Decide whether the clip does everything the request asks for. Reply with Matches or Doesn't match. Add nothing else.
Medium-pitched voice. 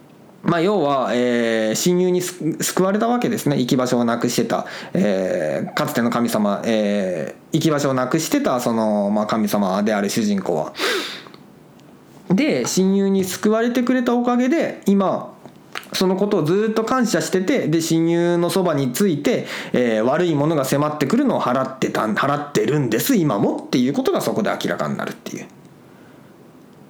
Matches